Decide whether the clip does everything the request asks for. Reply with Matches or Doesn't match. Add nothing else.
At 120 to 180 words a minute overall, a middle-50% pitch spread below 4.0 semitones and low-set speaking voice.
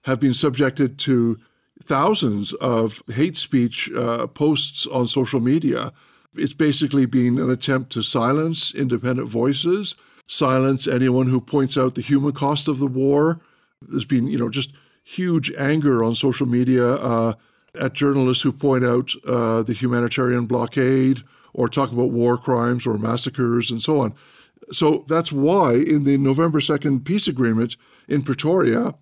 Matches